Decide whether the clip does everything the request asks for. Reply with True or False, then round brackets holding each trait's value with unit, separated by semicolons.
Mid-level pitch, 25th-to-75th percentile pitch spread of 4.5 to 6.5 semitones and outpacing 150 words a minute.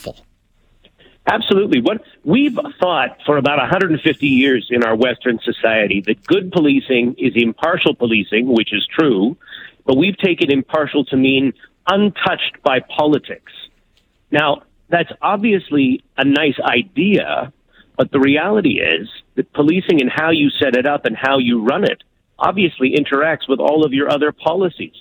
False (145 Hz; 5.3 semitones; 145 wpm)